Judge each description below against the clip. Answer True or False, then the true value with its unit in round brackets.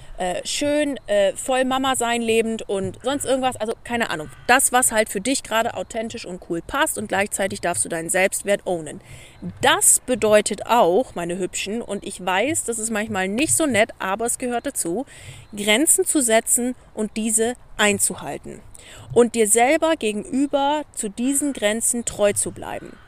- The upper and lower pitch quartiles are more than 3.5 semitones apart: True (4.6 semitones)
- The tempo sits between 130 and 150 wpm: False (160 wpm)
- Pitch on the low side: False (225 Hz)